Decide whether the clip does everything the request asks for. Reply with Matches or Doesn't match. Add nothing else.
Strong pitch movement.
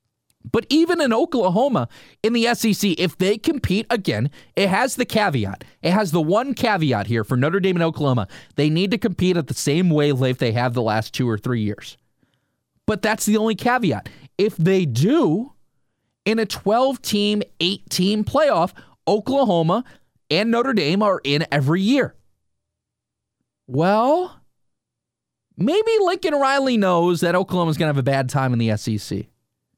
Matches